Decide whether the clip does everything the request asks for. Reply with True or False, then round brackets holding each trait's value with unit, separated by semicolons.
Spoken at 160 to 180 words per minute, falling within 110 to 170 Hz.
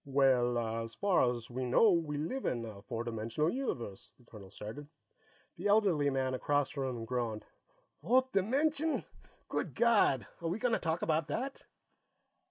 True (165 wpm; 140 Hz)